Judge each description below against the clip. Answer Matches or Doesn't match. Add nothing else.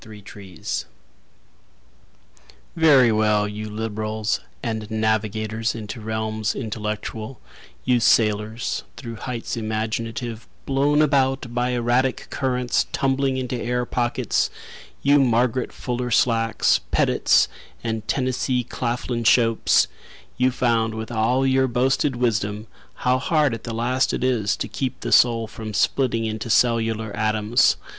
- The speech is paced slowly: Matches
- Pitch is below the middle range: Matches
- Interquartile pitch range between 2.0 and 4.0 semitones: Matches